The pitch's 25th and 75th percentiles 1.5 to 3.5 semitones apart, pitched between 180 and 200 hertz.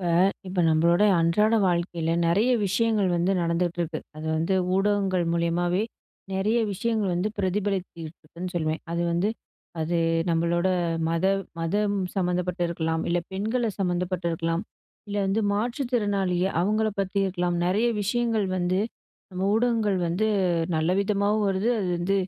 Yes: average, 3.2 semitones; medium, 185 Hz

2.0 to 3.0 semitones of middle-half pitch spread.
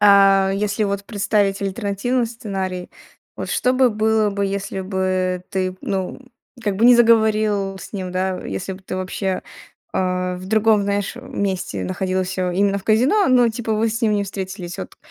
Yes: narrow, 2.6 semitones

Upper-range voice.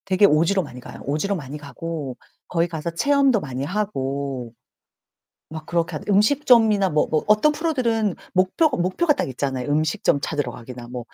No: medium, 165 Hz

